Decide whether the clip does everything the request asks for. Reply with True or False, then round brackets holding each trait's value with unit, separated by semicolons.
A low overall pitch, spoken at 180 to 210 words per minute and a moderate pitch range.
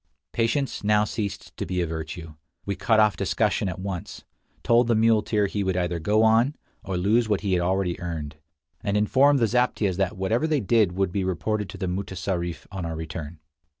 True (100 Hz; 195 wpm; 3.7 semitones)